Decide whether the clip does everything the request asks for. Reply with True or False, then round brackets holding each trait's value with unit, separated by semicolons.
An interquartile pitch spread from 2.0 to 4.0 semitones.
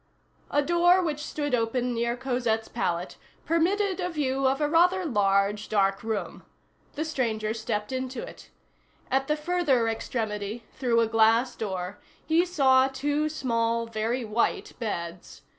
False (5.3 semitones)